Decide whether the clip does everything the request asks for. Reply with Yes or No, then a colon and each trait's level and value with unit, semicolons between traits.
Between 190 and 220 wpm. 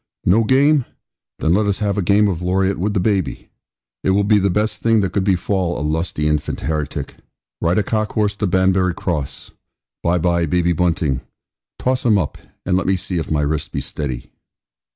Yes: average, 195 wpm